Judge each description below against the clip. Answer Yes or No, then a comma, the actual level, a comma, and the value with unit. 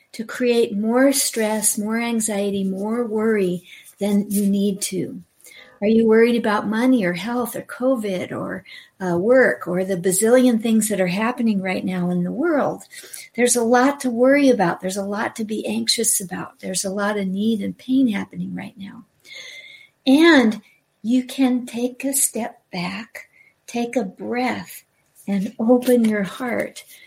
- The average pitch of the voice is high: Yes, high, 225 Hz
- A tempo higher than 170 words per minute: No, average, 160 wpm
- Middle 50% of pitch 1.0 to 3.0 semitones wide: No, average, 3.7 semitones